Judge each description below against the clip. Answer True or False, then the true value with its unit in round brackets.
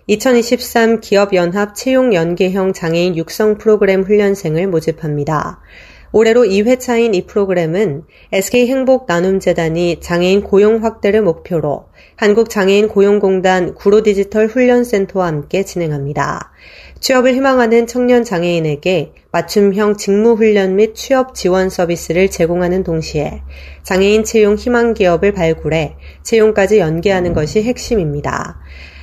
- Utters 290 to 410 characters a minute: True (310 characters per minute)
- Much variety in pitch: False (4.5 semitones)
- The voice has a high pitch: True (195 Hz)